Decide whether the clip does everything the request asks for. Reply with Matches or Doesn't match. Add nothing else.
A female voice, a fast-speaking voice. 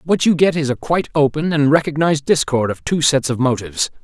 Doesn't match